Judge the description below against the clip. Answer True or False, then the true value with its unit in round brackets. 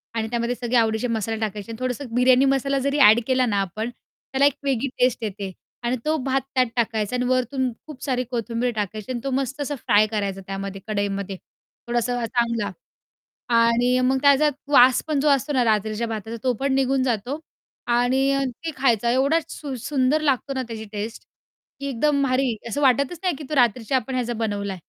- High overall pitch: True (245 Hz)